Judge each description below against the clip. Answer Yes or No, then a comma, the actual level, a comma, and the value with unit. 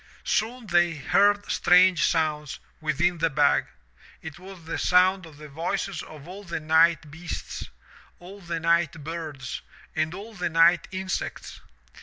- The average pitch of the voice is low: No, medium, 170 Hz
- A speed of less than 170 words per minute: Yes, average, 145 wpm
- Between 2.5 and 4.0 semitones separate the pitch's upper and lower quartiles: Yes, average, 2.8 semitones